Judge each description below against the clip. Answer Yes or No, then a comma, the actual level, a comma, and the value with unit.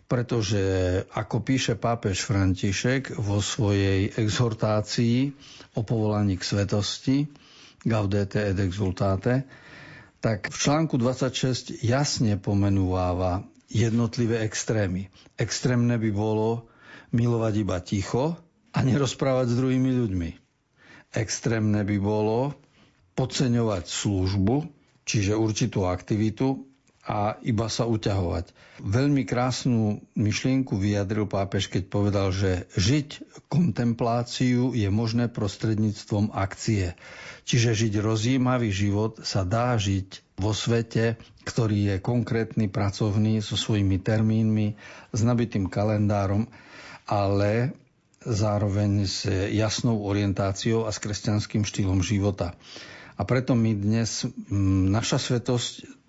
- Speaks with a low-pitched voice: Yes, low, 110 Hz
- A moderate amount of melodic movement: Yes, average, 3.4 semitones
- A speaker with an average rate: No, slow, 105 wpm